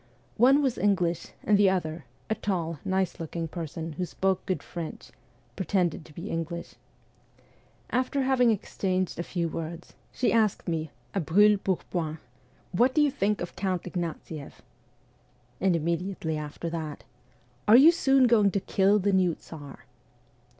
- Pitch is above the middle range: No, medium, 180 Hz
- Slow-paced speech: No, average, 155 wpm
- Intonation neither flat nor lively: Yes, average, 4.0 semitones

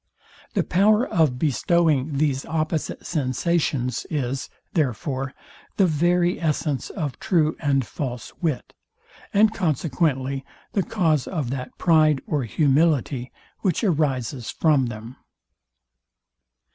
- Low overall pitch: No, medium, 150 Hz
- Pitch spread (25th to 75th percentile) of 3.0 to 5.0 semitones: Yes, average, 4.2 semitones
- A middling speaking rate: No, slow, 110 wpm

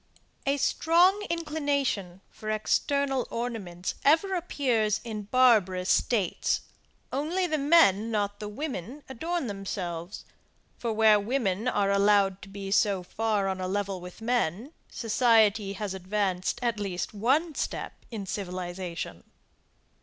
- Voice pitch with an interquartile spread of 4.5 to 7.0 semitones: Yes, wide, 5.4 semitones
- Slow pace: Yes, slow, 125 wpm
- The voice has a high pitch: Yes, high, 215 Hz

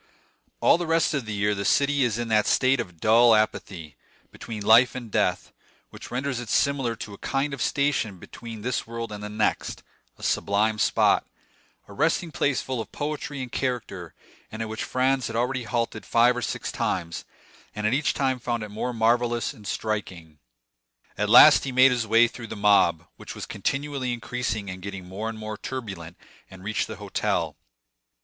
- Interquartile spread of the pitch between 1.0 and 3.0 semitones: No, average, 3.6 semitones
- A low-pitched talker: Yes, low, 115 Hz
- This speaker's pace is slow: No, average, 185 wpm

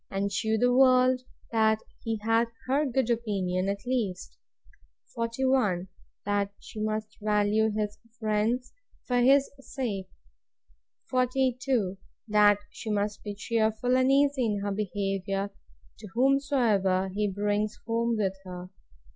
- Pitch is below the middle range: No, high, 220 Hz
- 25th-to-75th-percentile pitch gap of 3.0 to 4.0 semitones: Yes, average, 3.6 semitones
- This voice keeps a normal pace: No, slow, 125 wpm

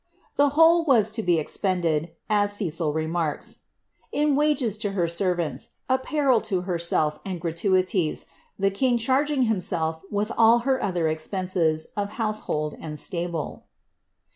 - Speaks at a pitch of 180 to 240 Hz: Yes, high, 190 Hz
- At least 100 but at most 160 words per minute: Yes, average, 140 wpm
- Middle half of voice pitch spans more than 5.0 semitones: Yes, wide, 5.6 semitones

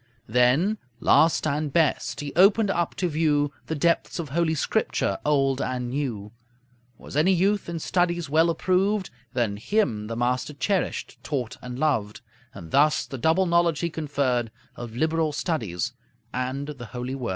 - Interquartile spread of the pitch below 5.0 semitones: No, average, 5.3 semitones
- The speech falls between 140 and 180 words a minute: Yes, average, 160 wpm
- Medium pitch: Yes, medium, 150 Hz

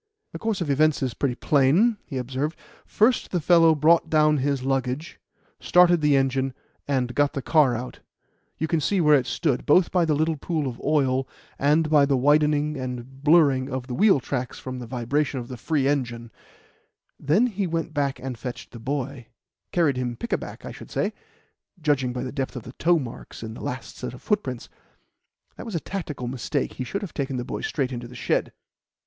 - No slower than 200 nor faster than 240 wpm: Yes, fast, 205 wpm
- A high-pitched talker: No, medium, 140 Hz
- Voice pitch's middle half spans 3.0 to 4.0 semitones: Yes, average, 3.6 semitones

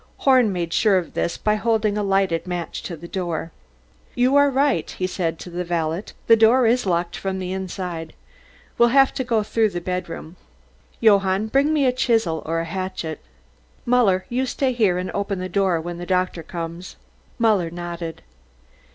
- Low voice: No, high, 190 Hz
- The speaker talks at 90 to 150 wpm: No, average, 180 wpm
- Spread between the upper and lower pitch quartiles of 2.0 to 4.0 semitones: No, average, 4.6 semitones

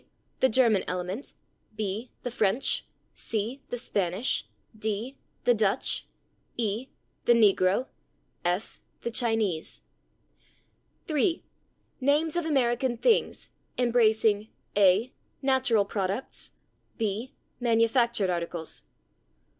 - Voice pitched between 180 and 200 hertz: No, high, 225 Hz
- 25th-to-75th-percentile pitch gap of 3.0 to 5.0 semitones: Yes, average, 4.0 semitones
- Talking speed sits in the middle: No, slow, 90 wpm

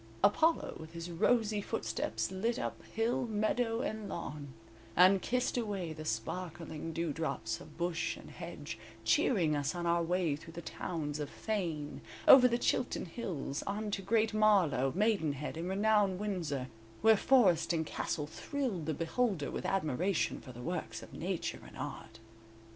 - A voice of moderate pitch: Yes, medium, 175 Hz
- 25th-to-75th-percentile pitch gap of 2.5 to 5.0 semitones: No, wide, 5.5 semitones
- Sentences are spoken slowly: No, average, 155 wpm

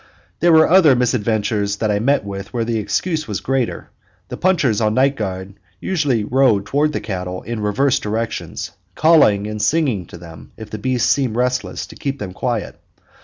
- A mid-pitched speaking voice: No, low, 115 Hz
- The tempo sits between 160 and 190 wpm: Yes, average, 180 wpm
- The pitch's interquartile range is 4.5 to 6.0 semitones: Yes, average, 5.0 semitones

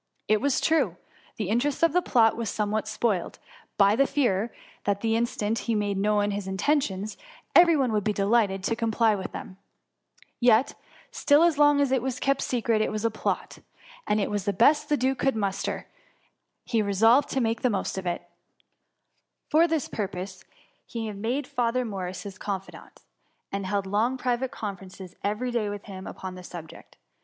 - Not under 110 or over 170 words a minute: No, average, 185 wpm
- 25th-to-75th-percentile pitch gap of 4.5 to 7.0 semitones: No, average, 4.1 semitones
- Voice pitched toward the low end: No, high, 220 Hz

